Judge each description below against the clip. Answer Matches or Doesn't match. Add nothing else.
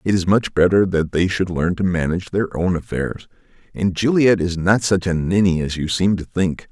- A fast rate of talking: Matches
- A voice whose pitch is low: Matches